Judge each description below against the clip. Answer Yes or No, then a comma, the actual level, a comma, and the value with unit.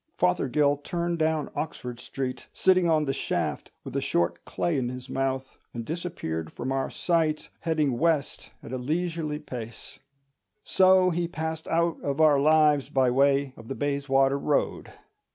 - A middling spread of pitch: Yes, average, 3.6 semitones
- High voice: No, medium, 145 Hz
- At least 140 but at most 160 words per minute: Yes, average, 155 wpm